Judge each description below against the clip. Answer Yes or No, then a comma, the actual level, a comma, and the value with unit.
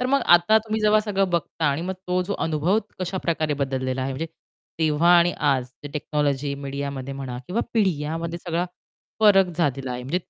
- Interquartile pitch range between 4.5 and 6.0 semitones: Yes, average, 5.1 semitones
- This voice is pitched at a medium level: Yes, medium, 160 Hz